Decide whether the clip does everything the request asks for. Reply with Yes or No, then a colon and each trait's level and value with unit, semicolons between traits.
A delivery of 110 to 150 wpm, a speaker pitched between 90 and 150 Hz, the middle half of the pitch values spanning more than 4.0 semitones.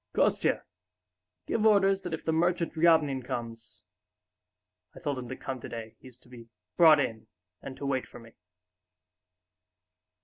Yes: average, 145 wpm; low, 135 Hz; wide, 5.6 semitones